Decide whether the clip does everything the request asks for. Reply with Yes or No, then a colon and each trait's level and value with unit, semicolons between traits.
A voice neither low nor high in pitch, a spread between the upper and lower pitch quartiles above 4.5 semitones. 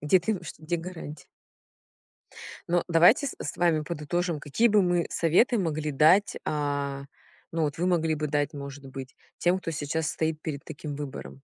No: medium, 155 Hz; average, 3.2 semitones